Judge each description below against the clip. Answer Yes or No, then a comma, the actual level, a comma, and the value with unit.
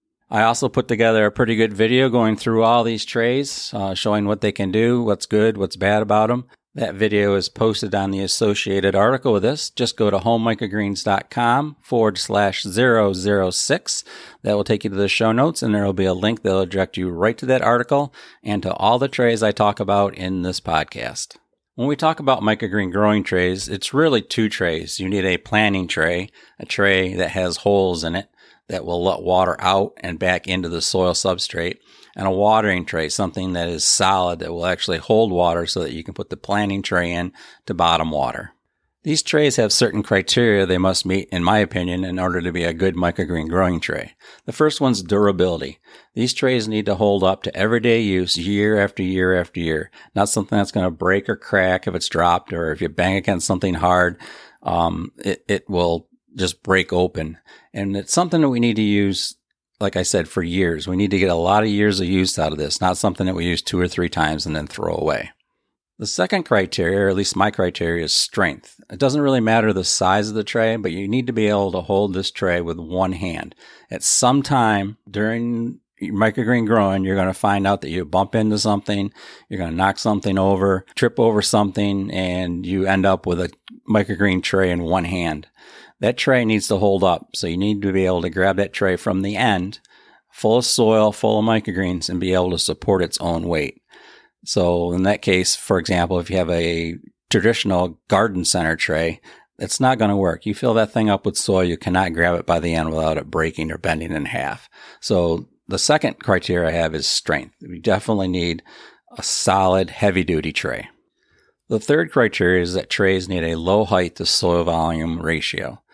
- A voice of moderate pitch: No, very low, 95 Hz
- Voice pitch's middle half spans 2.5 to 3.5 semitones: Yes, average, 3.1 semitones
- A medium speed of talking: No, fast, 210 wpm